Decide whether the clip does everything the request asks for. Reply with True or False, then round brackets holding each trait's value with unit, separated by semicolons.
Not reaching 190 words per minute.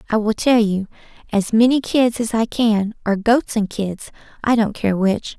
False (200 wpm)